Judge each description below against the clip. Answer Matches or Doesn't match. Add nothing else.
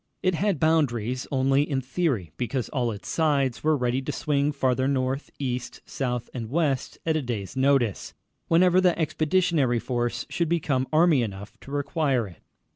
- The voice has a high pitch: Doesn't match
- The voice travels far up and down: Doesn't match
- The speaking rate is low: Doesn't match